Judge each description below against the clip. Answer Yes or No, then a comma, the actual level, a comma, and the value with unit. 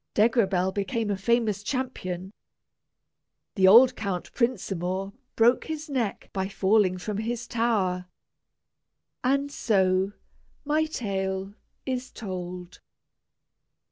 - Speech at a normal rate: No, slow, 100 wpm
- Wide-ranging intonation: No, average, 4.1 semitones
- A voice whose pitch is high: Yes, high, 205 Hz